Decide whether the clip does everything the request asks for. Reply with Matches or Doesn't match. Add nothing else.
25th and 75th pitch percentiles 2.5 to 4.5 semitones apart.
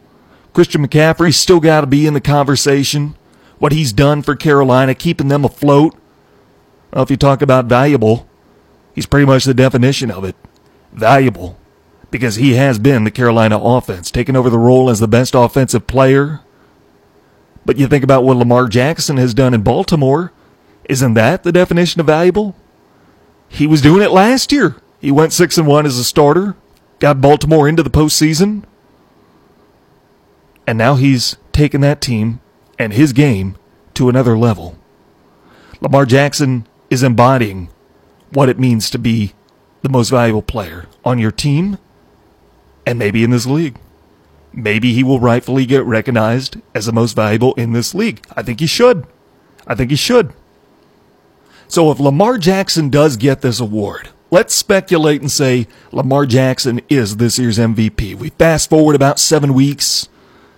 Matches